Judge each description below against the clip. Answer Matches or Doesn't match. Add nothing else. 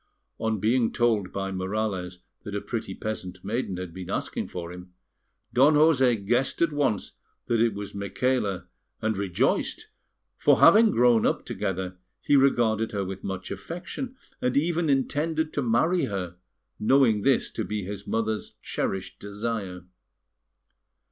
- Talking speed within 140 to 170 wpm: Matches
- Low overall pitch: Matches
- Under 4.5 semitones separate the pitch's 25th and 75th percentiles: Doesn't match